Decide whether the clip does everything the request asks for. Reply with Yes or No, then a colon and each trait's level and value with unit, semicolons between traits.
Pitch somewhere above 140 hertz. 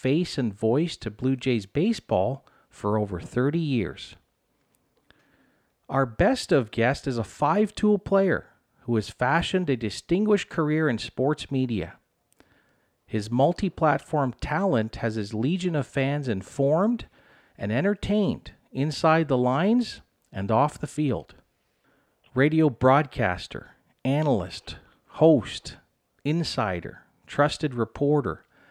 No: low, 135 Hz